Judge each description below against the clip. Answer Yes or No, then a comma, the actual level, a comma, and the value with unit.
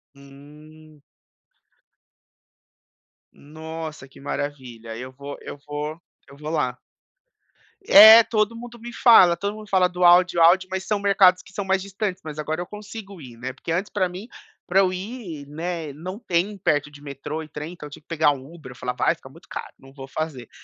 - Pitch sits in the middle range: Yes, medium, 165 Hz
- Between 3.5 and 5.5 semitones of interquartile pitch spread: Yes, average, 4.8 semitones